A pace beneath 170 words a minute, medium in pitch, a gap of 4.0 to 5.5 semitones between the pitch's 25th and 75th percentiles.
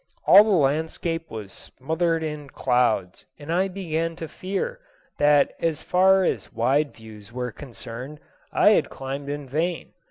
Yes: average, 150 wpm; medium, 150 Hz; average, 4.6 semitones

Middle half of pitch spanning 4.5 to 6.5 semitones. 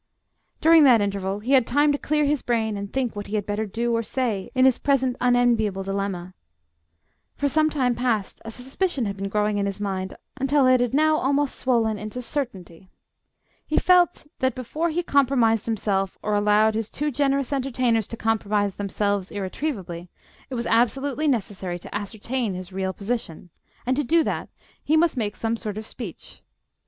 Yes: average, 4.8 semitones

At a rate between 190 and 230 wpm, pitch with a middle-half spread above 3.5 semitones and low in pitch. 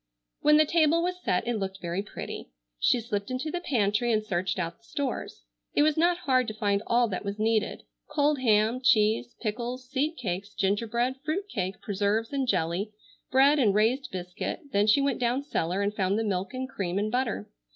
No: average, 195 wpm; average, 4.9 semitones; high, 225 Hz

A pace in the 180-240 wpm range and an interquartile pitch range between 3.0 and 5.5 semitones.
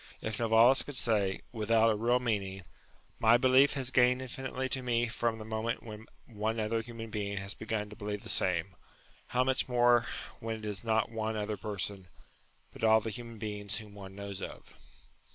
No: average, 195 wpm; narrow, 2.4 semitones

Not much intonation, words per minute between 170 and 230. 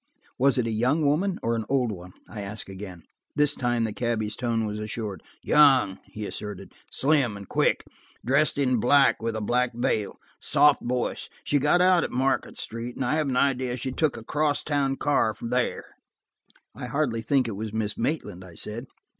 No: average, 4.3 semitones; average, 190 wpm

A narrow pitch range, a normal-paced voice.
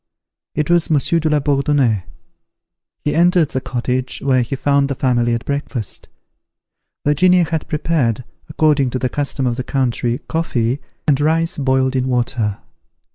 No: average, 3.4 semitones; average, 150 wpm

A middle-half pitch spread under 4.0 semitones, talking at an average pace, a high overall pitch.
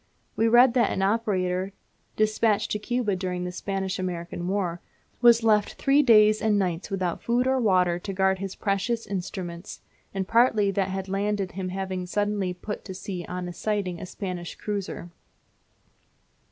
Yes: average, 2.7 semitones; average, 160 wpm; high, 195 Hz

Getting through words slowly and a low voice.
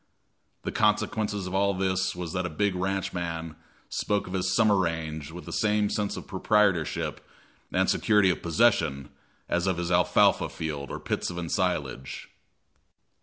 No: average, 155 wpm; very low, 90 Hz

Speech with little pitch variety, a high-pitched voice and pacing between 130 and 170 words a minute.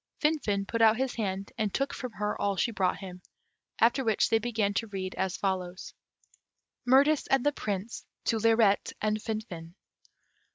No: average, 3.3 semitones; high, 215 Hz; average, 165 wpm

